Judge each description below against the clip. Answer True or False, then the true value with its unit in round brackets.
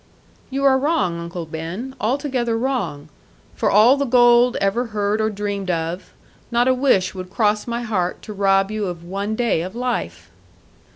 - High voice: True (210 Hz)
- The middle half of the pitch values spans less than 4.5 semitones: False (4.9 semitones)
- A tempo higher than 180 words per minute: False (170 wpm)